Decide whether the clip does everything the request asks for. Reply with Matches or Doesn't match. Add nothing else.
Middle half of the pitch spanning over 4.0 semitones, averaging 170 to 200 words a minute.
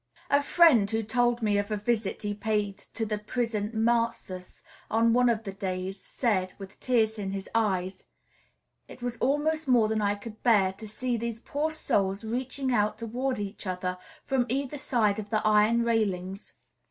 Doesn't match